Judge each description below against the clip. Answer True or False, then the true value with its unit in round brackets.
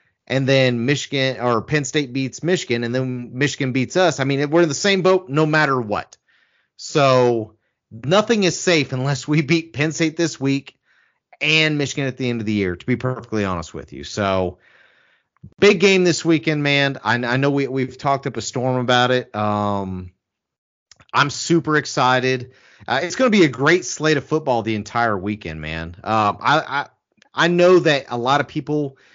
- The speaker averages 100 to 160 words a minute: False (190 wpm)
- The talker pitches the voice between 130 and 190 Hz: True (135 Hz)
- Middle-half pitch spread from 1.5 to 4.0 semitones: False (4.6 semitones)